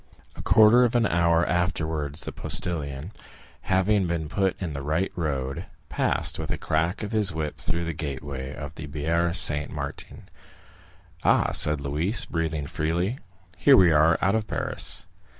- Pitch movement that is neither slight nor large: Yes, average, 3.9 semitones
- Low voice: Yes, very low, 80 Hz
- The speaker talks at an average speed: Yes, average, 160 wpm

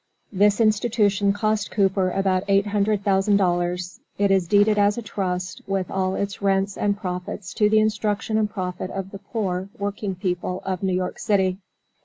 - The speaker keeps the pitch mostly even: Yes, narrow, 1.8 semitones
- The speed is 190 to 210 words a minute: No, average, 175 wpm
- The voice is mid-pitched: No, high, 195 Hz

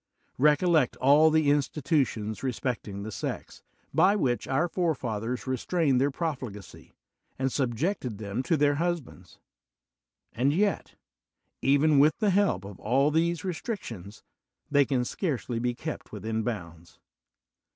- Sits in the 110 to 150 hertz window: Yes, low, 135 Hz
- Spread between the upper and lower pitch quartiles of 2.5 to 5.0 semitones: No, wide, 5.6 semitones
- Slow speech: Yes, slow, 130 wpm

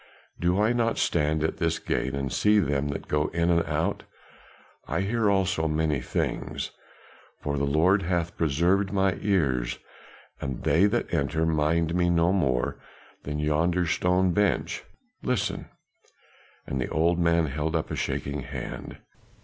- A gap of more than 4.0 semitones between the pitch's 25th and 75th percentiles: No, average, 3.6 semitones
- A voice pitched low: Yes, very low, 85 Hz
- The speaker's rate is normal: Yes, average, 150 wpm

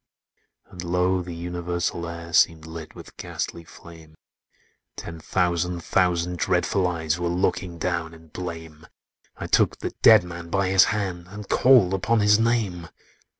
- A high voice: No, very low, 90 Hz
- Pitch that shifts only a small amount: Yes, narrow, 1.7 semitones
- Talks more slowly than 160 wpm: Yes, average, 150 wpm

